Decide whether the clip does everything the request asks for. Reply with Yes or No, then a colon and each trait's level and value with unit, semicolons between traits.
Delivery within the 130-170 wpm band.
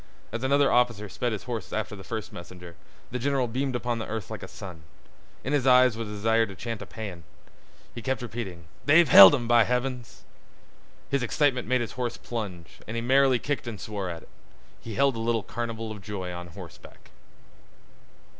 No: average, 195 wpm